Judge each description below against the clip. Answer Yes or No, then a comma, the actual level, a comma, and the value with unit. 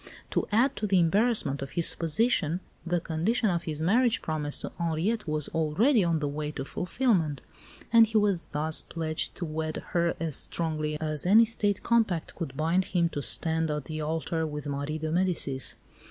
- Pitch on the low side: No, medium, 165 Hz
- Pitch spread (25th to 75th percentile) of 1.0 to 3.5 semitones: No, average, 4.2 semitones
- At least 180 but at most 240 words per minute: Yes, average, 185 wpm